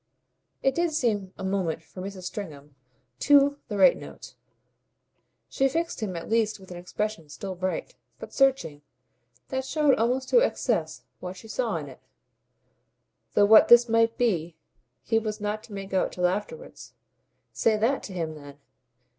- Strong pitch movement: Yes, wide, 5.9 semitones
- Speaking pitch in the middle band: No, high, 210 Hz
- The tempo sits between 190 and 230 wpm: No, average, 165 wpm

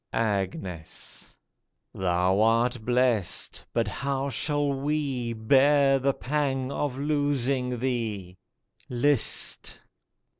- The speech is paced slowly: Yes, slow, 90 wpm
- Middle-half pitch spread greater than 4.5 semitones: No, average, 4.0 semitones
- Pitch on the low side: Yes, low, 125 Hz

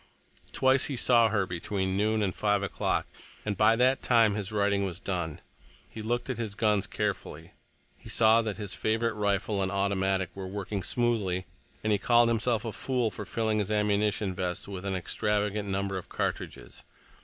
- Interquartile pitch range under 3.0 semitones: Yes, narrow, 2.5 semitones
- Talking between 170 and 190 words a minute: Yes, average, 180 wpm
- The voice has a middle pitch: No, low, 105 Hz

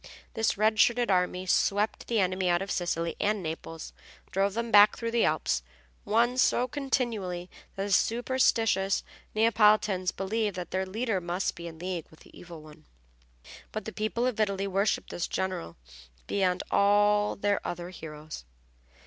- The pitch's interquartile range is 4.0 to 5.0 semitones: No, average, 3.4 semitones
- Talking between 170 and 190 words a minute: No, average, 155 wpm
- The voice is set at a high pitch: Yes, high, 200 Hz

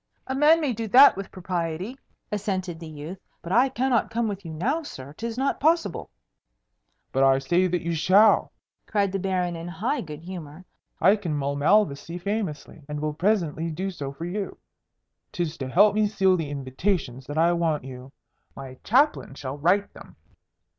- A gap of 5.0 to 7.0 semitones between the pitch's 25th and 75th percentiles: Yes, wide, 5.4 semitones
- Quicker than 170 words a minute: Yes, average, 180 wpm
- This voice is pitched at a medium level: Yes, medium, 180 Hz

